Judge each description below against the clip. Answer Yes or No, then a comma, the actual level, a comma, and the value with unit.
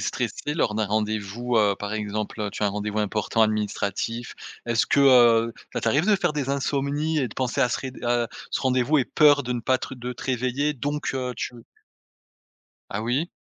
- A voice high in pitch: No, low, 120 Hz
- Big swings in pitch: No, average, 4.3 semitones